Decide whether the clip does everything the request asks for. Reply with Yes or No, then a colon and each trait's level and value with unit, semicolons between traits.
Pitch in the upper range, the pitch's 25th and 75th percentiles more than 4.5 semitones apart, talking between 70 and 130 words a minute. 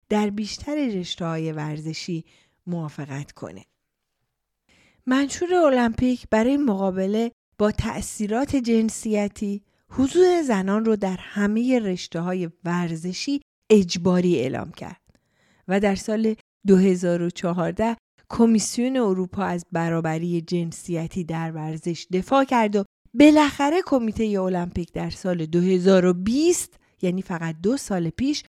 Yes: high, 195 Hz; average, 5.0 semitones; slow, 105 wpm